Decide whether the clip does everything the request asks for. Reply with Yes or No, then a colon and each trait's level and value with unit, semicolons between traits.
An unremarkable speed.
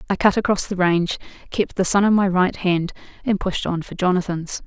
No: fast, 220 wpm